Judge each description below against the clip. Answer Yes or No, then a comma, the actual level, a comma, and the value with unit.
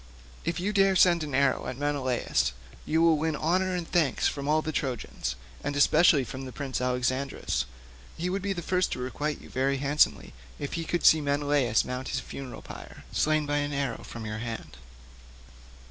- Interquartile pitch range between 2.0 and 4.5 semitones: Yes, average, 3.9 semitones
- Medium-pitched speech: Yes, medium, 145 Hz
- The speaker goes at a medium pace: Yes, average, 180 wpm